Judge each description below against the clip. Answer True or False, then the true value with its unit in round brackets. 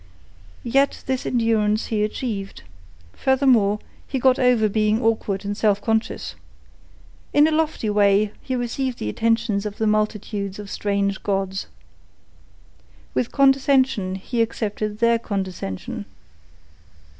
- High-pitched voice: True (215 Hz)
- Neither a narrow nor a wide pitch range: True (3.6 semitones)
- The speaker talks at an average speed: False (120 wpm)